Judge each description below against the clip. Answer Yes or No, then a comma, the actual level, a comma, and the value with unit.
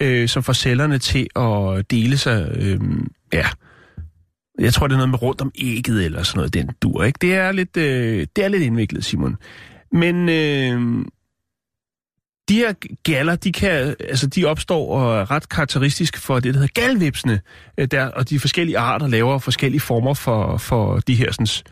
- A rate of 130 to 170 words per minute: No, average, 180 wpm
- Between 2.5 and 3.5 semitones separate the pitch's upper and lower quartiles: No, average, 4.1 semitones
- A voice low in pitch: Yes, low, 130 Hz